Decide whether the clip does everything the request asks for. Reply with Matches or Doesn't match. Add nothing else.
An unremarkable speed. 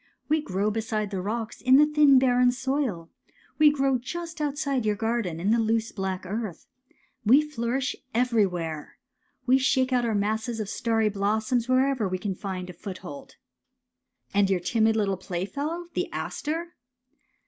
Matches